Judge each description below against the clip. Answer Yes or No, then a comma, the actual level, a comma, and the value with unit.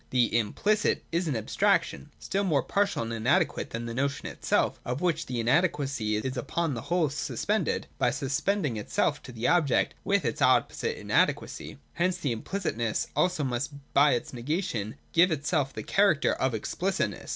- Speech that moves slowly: No, average, 165 wpm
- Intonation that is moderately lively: No, wide, 6.6 semitones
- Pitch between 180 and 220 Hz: No, medium, 140 Hz